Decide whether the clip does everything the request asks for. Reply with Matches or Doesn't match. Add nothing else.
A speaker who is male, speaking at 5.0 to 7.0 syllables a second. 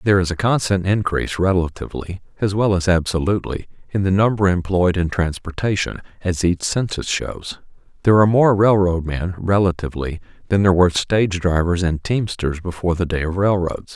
Matches